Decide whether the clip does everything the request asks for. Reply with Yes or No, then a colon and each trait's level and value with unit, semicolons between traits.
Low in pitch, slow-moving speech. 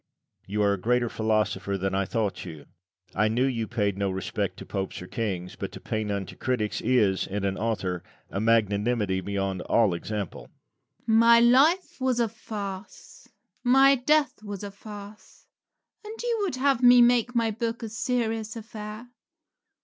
No: low, 120 Hz; average, 170 wpm